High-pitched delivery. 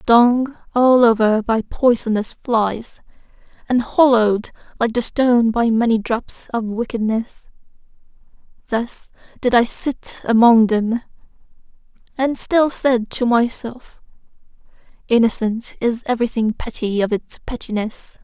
Yes: high, 235 Hz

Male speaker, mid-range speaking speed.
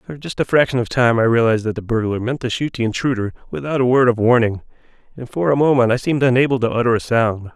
No: male; fast, 255 wpm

